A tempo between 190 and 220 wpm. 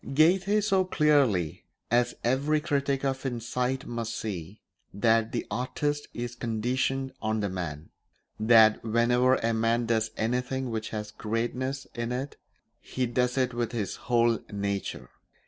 No: average, 140 wpm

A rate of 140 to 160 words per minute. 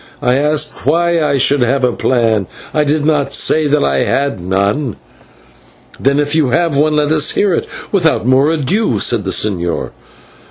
No: average, 175 wpm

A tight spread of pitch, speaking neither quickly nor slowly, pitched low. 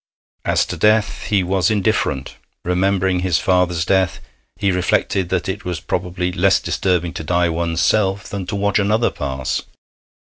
Yes: narrow, 2.1 semitones; average, 155 wpm; very low, 95 Hz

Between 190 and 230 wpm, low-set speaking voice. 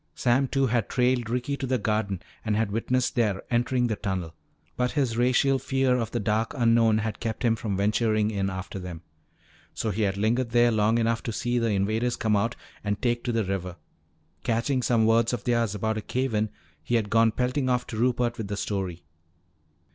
Yes: fast, 205 wpm; low, 115 Hz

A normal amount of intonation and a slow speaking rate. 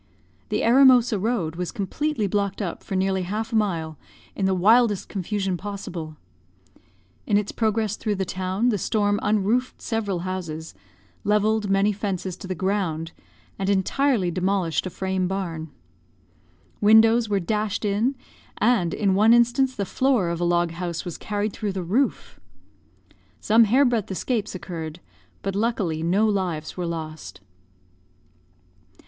No: average, 3.4 semitones; average, 145 wpm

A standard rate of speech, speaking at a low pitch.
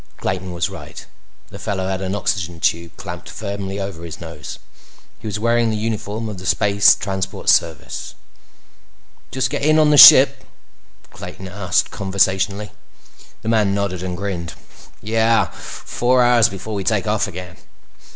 Yes: average, 150 wpm; low, 100 Hz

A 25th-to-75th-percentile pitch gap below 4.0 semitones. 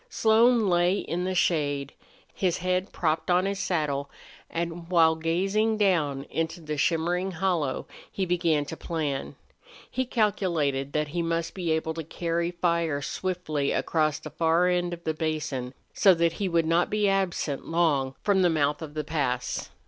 Yes: average, 3.0 semitones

